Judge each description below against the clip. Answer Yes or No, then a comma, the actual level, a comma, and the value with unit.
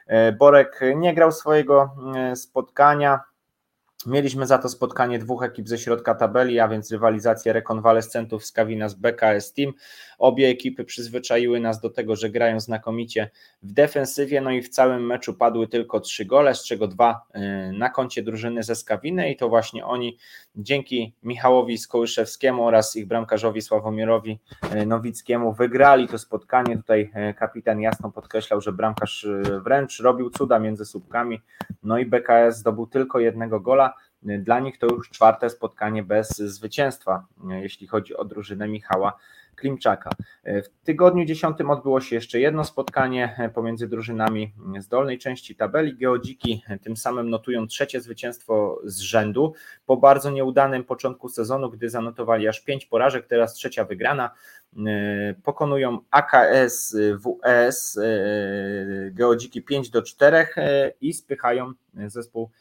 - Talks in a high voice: No, low, 115 Hz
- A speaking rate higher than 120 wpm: Yes, average, 135 wpm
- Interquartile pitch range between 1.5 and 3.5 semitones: Yes, average, 2.9 semitones